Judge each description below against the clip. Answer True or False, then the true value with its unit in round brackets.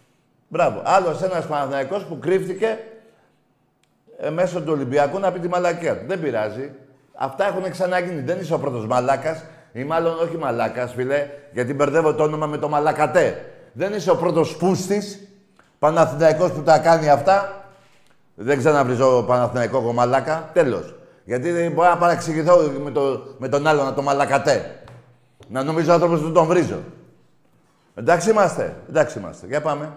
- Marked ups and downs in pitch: False (4.2 semitones)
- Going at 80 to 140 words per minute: False (155 wpm)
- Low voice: False (160 Hz)